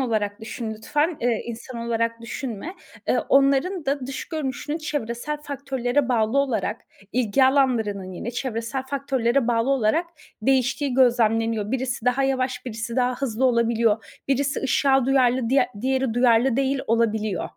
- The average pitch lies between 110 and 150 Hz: No, very high, 250 Hz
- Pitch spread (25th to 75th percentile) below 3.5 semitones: Yes, average, 2.9 semitones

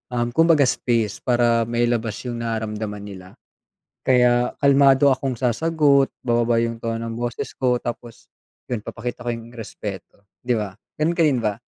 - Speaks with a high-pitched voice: No, low, 120 Hz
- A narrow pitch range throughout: Yes, narrow, 2.2 semitones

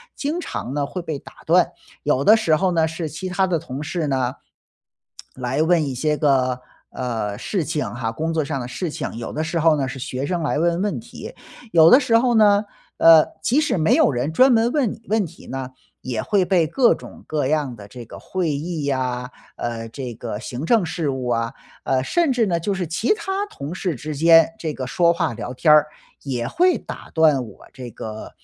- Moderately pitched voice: Yes, medium, 155 Hz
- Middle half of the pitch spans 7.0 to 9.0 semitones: No, wide, 5.9 semitones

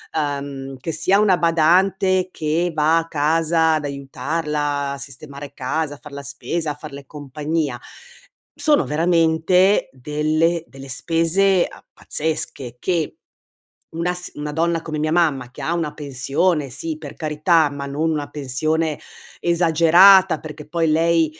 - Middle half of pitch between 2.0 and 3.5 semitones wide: Yes, narrow, 2.6 semitones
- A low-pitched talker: No, medium, 155 Hz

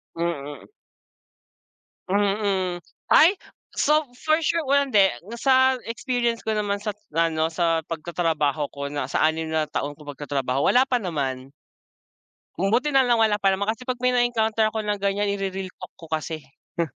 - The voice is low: No, high, 195 Hz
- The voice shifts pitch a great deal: Yes, wide, 6.6 semitones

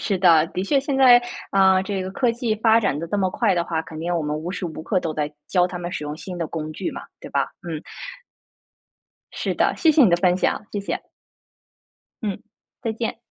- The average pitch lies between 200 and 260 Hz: No, medium, 185 Hz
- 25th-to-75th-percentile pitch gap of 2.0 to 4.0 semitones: No, average, 4.6 semitones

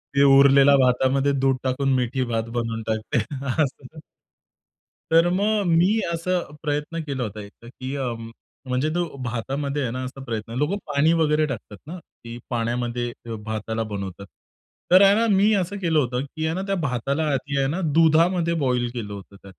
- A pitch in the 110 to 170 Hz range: Yes, low, 135 Hz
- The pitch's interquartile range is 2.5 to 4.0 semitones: No, average, 5.1 semitones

